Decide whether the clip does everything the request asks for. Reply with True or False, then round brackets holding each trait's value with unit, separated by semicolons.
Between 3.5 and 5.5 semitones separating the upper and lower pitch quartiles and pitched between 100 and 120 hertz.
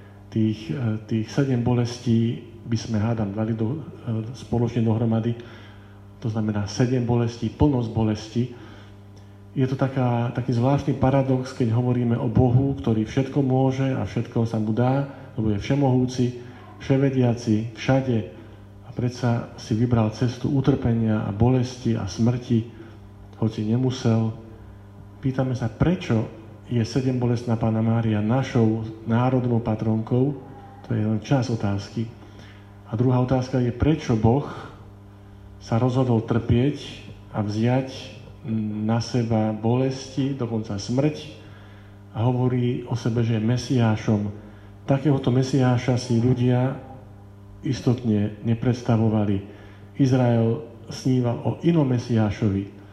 False (2.8 semitones; 115 Hz)